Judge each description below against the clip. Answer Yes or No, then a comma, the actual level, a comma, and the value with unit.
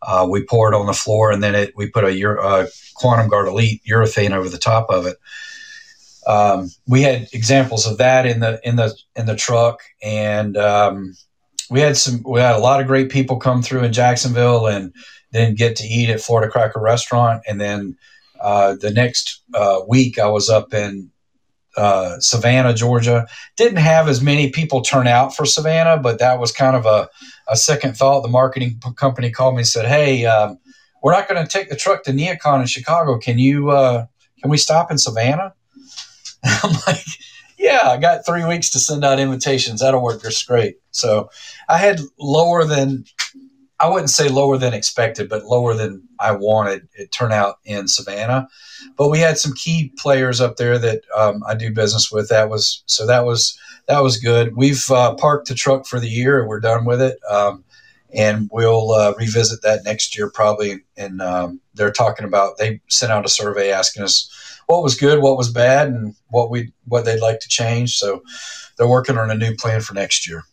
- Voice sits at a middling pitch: No, low, 120 Hz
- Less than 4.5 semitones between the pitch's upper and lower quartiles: Yes, average, 4.1 semitones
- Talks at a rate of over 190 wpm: Yes, average, 200 wpm